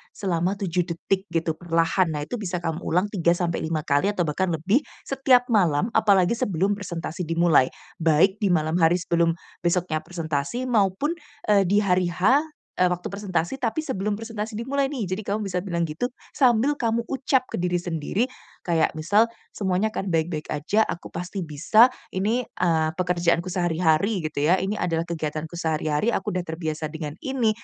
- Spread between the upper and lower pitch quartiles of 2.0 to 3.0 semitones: No, average, 4.0 semitones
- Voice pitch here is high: No, medium, 180 Hz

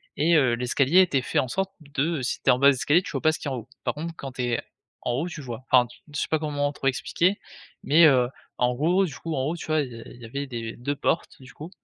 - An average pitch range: Yes, average, 3.9 semitones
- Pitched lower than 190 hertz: Yes, medium, 140 Hz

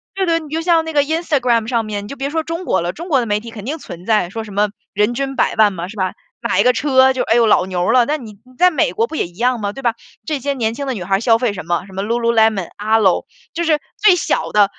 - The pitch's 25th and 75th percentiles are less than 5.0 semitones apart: No, wide, 5.5 semitones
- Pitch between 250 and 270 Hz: No, high, 235 Hz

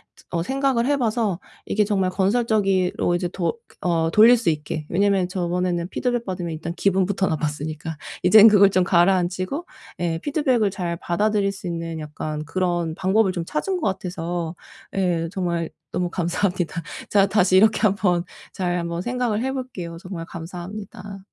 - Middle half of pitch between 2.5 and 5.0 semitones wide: Yes, average, 3.4 semitones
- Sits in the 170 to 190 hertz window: Yes, medium, 185 Hz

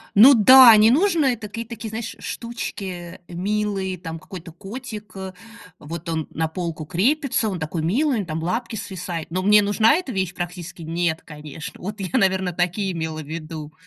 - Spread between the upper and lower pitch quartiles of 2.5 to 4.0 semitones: No, average, 4.7 semitones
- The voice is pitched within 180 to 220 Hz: Yes, high, 190 Hz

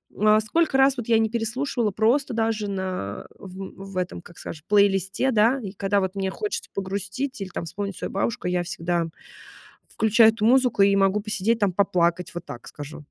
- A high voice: Yes, high, 200 Hz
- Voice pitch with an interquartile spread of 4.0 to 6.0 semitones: No, average, 3.2 semitones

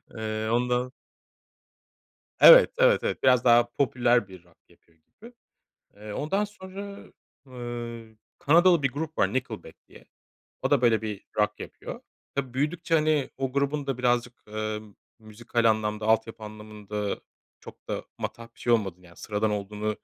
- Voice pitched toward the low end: Yes, low, 120 Hz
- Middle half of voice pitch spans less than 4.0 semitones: No, average, 4.4 semitones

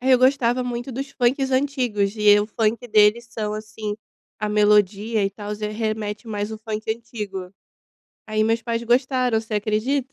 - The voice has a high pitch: Yes, high, 220 Hz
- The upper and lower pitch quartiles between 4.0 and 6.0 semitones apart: No, narrow, 2.5 semitones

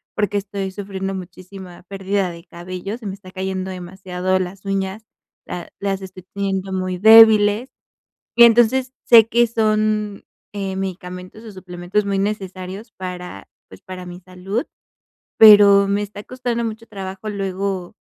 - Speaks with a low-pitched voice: No, high, 195 Hz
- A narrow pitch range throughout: Yes, narrow, 2.2 semitones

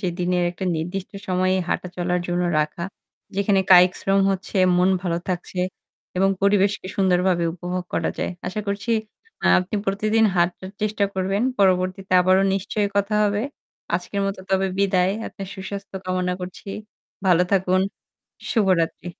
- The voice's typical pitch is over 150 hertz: Yes, medium, 185 Hz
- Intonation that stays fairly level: Yes, narrow, 1.6 semitones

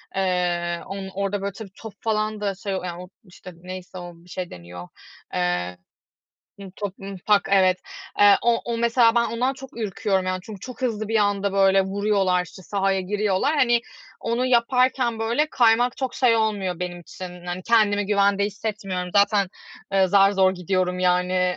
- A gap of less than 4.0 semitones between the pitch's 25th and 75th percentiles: Yes, average, 3.3 semitones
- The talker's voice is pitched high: Yes, high, 195 Hz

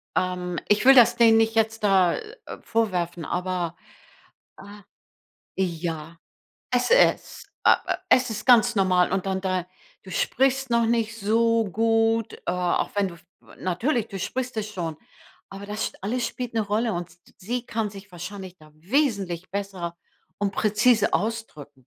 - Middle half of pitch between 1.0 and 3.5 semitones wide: No, average, 4.0 semitones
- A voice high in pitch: Yes, high, 205 Hz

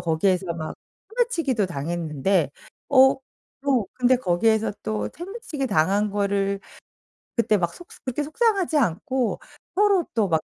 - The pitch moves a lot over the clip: Yes, wide, 7.9 semitones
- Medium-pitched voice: No, high, 220 Hz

